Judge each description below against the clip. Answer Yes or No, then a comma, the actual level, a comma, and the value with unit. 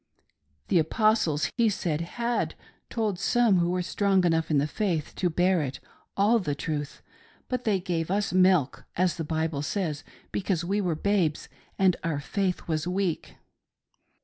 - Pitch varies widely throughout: No, average, 3.9 semitones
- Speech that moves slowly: No, average, 160 wpm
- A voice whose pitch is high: No, medium, 180 Hz